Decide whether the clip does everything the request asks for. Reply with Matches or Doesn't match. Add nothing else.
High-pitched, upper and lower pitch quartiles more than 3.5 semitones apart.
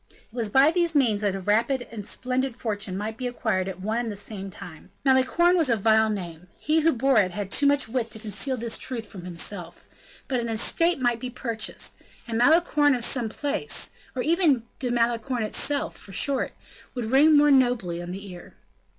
Matches